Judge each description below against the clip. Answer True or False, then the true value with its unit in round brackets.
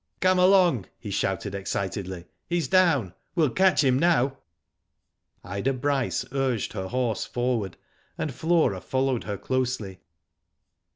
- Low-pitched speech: True (130 Hz)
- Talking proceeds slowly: True (120 wpm)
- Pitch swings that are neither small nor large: False (7.2 semitones)